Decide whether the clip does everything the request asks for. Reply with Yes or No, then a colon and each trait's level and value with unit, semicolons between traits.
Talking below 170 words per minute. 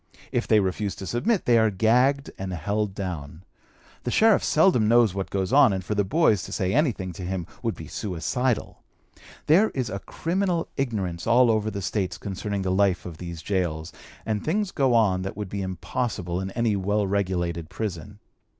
No: average, 185 wpm